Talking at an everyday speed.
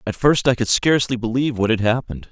No: fast, 235 wpm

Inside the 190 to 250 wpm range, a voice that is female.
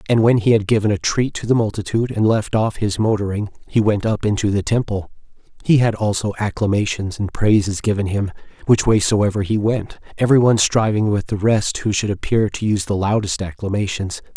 No: average, 200 wpm; male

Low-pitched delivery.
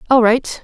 No: high, 240 Hz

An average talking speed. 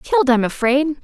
Yes: average, 175 wpm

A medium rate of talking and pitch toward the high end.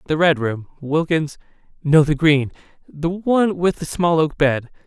No: average, 150 wpm; medium, 155 Hz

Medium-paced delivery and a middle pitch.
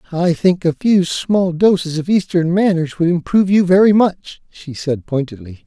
Yes: average, 180 wpm; medium, 170 Hz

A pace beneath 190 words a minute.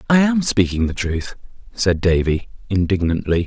Yes: average, 140 wpm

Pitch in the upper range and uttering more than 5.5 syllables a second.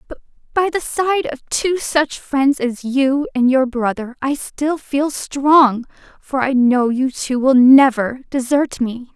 No: very high, 270 Hz; 3.7 syllables/s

